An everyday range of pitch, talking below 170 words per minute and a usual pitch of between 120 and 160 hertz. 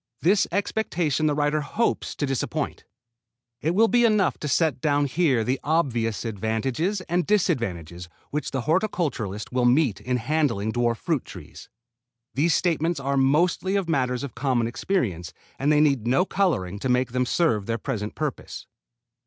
No: wide, 6.0 semitones; average, 160 wpm; medium, 140 Hz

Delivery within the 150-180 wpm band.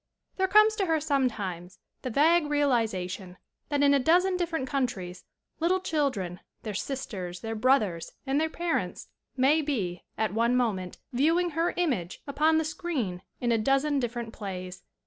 Yes: average, 160 wpm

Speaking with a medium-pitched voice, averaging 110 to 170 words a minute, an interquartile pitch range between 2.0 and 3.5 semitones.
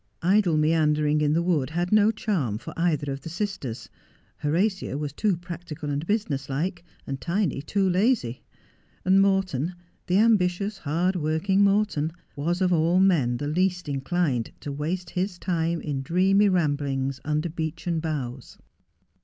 No: medium, 170 Hz; average, 145 wpm; average, 4.2 semitones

